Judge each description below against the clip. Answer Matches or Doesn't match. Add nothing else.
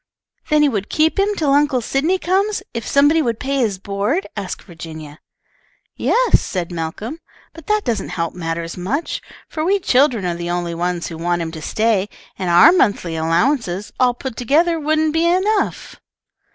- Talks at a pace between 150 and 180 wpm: Matches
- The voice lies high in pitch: Matches